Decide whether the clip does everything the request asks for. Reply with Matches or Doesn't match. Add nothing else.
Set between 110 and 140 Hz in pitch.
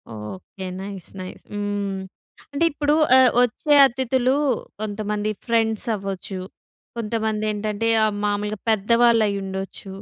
Doesn't match